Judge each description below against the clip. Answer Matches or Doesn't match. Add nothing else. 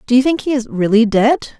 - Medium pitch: Doesn't match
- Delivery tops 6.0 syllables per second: Matches